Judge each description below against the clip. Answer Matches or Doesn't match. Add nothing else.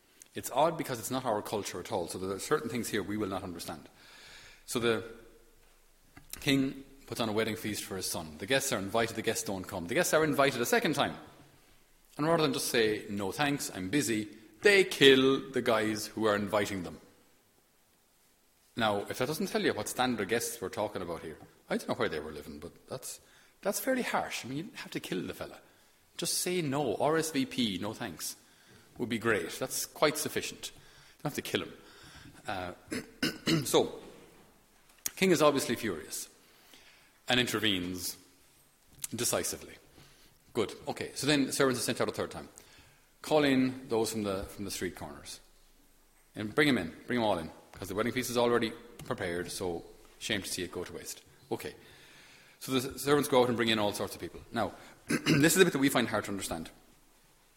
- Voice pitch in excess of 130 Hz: Doesn't match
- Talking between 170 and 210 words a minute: Matches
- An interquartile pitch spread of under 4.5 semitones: Doesn't match